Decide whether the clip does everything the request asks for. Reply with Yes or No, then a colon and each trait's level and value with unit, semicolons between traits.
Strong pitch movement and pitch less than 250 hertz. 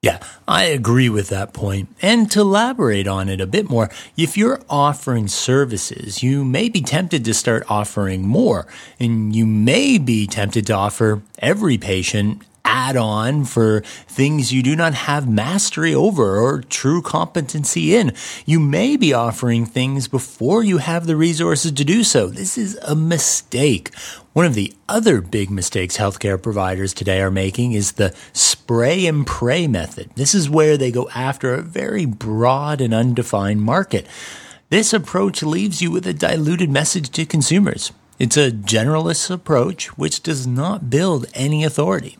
Yes: wide, 7.1 semitones; low, 135 Hz